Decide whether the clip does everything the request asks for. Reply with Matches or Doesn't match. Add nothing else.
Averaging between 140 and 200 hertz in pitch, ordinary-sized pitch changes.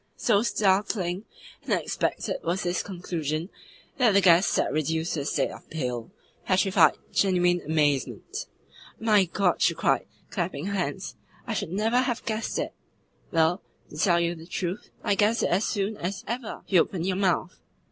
Matches